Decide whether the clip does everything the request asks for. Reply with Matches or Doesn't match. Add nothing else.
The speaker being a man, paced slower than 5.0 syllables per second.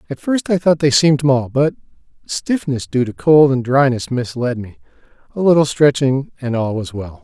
Doesn't match